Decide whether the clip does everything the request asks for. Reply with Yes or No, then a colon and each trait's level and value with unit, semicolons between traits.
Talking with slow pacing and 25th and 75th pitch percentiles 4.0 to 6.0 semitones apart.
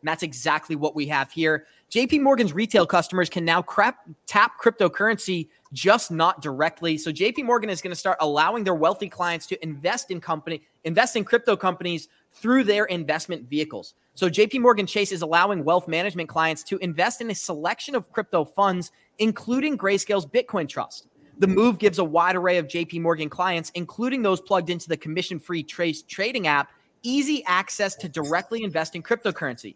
No: average, 180 wpm; average, 4.3 semitones